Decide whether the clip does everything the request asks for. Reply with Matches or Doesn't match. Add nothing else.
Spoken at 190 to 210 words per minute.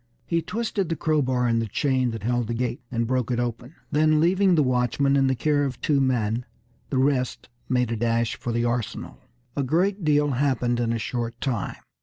Matches